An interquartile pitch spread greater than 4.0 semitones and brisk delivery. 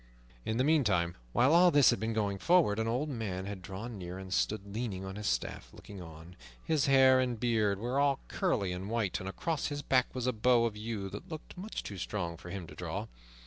Yes: wide, 5.4 semitones; fast, 225 wpm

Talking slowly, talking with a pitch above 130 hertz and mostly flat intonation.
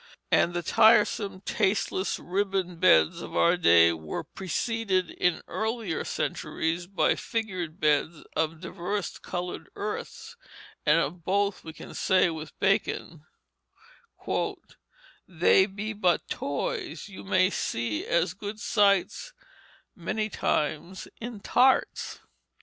No: slow, 115 wpm; medium, 185 Hz; average, 3.8 semitones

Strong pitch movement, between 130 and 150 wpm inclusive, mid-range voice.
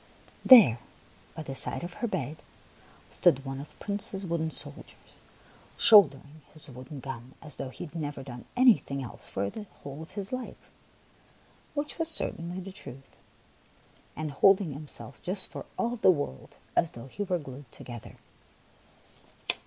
No: wide, 6.2 semitones; average, 160 wpm; medium, 155 Hz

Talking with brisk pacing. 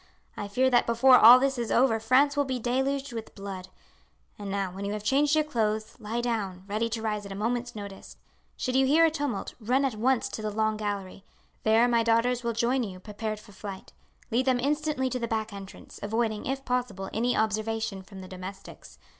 Yes: fast, 210 wpm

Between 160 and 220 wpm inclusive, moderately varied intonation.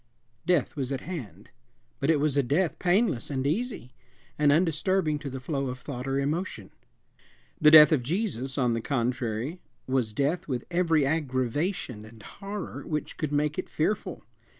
Yes: average, 165 wpm; average, 4.3 semitones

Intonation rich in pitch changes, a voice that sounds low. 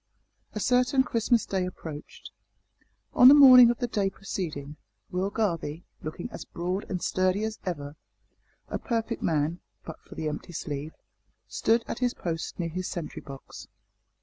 No: wide, 6.2 semitones; medium, 185 Hz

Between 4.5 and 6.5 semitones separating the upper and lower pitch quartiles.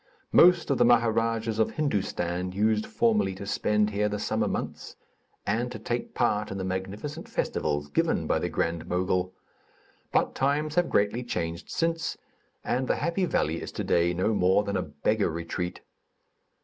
Yes: average, 5.0 semitones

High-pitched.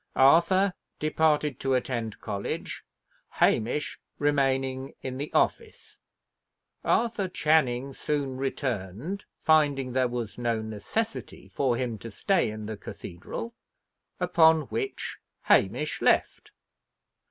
No: low, 135 Hz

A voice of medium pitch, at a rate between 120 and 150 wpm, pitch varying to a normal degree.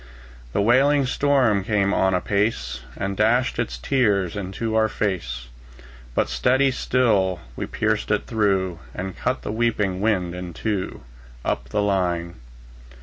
No: low, 100 Hz; average, 140 wpm; average, 3.8 semitones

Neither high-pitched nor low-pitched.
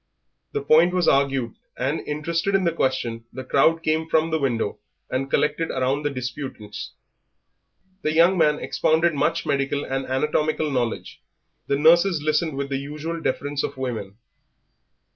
Yes: medium, 145 Hz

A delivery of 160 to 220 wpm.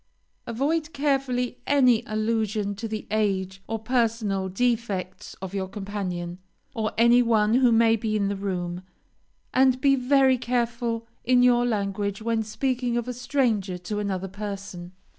No: average, 145 wpm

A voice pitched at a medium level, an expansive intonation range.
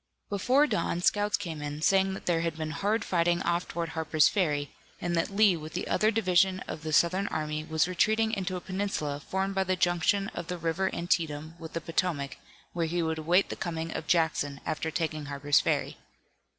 No: medium, 170 Hz; average, 3.2 semitones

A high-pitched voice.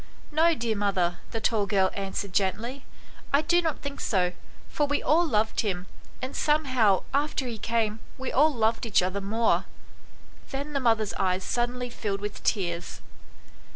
Yes: high, 225 Hz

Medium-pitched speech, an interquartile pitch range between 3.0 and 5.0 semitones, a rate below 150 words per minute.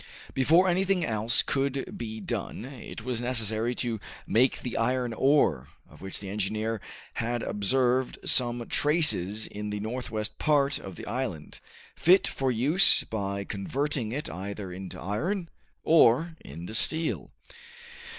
No: low, 120 Hz; average, 4.7 semitones; slow, 135 wpm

